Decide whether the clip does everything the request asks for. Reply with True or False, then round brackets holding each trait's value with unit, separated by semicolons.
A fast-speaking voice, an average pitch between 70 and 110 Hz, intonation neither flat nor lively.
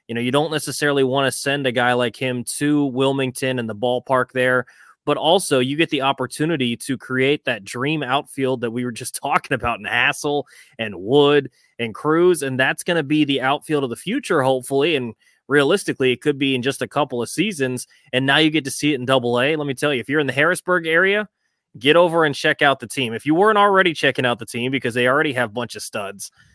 False (240 wpm; 135 Hz; 3.0 semitones)